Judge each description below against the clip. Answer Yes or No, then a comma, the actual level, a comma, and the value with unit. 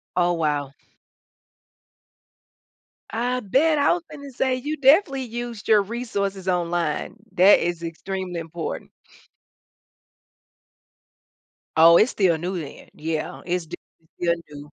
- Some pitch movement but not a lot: No, wide, 6.6 semitones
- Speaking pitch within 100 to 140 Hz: No, high, 190 Hz